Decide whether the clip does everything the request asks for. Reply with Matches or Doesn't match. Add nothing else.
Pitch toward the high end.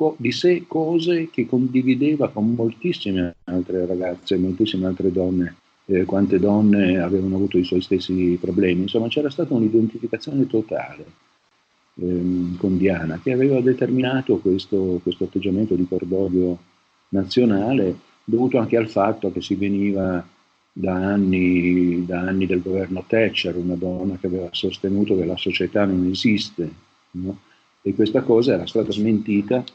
Doesn't match